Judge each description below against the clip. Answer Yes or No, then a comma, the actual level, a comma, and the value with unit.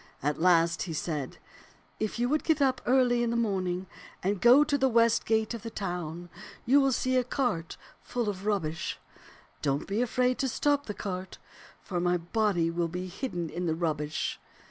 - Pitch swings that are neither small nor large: No, wide, 6.1 semitones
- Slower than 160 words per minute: No, average, 190 wpm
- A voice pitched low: No, high, 200 Hz